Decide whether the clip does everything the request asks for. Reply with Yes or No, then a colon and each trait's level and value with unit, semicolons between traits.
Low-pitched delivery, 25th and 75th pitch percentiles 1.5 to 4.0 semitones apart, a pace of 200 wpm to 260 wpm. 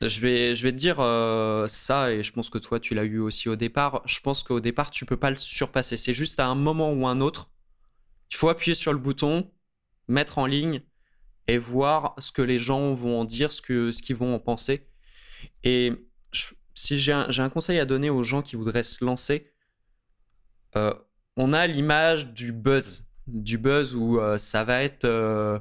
Yes: low, 125 Hz; average, 3.5 semitones; average, 215 wpm